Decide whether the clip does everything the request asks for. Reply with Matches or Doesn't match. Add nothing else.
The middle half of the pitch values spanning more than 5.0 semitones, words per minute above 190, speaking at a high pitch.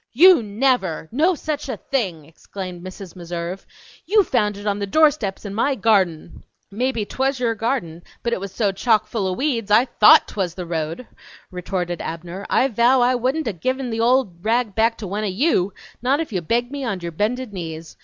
Matches